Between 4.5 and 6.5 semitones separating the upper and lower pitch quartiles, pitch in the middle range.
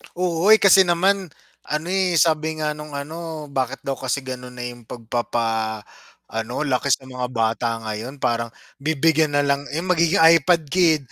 Yes: average, 4.9 semitones; medium, 145 Hz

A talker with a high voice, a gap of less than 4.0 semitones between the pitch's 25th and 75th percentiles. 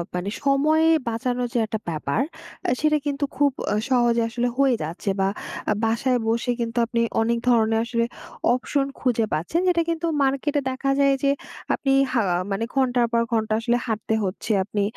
Yes: high, 240 Hz; average, 3.5 semitones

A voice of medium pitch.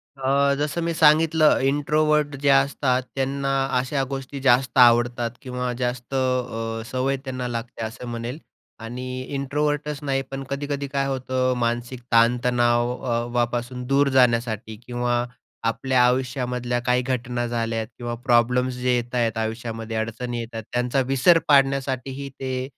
No: low, 125 Hz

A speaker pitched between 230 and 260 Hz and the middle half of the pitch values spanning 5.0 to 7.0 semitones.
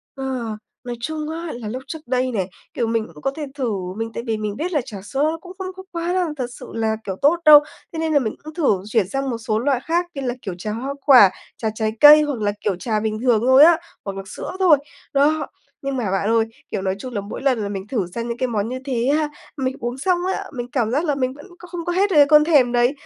Yes: very high, 255 Hz; average, 5.3 semitones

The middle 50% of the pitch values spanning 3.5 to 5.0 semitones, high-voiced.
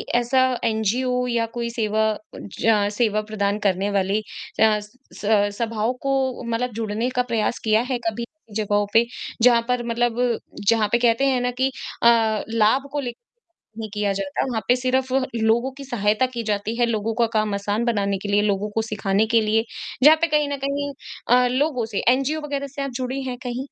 No: average, 2.9 semitones; high, 230 Hz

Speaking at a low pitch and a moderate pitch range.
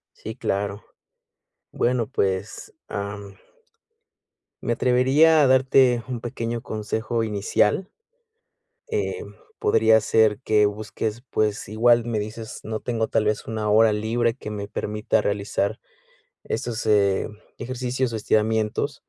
No: low, 110 Hz; narrow, 2.3 semitones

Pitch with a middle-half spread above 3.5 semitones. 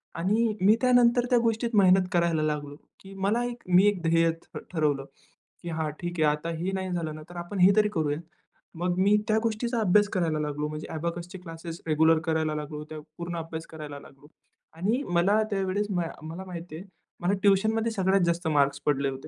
Yes: average, 4.1 semitones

